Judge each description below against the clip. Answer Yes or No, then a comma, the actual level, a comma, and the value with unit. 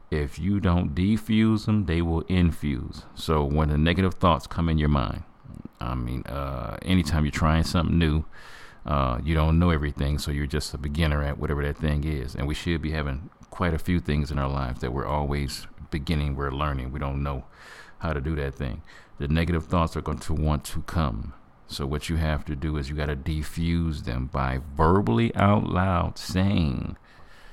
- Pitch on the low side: Yes, very low, 75 Hz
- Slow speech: No, average, 200 wpm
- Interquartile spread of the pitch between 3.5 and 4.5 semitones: No, average, 2.9 semitones